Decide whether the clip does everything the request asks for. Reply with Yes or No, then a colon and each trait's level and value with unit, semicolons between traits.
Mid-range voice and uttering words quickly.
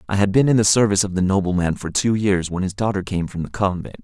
No: low, 100 Hz; fast, 280 wpm